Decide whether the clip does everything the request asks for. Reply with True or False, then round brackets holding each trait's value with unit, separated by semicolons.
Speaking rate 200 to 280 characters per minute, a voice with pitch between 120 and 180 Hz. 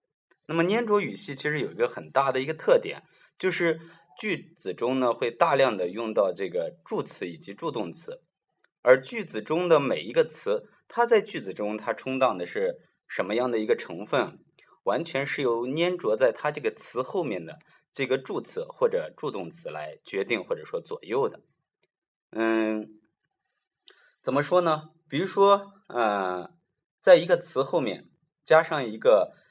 False (240 characters per minute; 205 Hz)